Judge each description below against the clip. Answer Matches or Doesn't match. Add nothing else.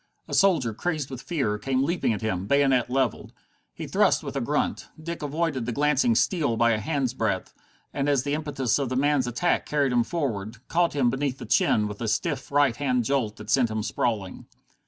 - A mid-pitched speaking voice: Doesn't match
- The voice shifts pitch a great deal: Doesn't match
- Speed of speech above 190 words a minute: Matches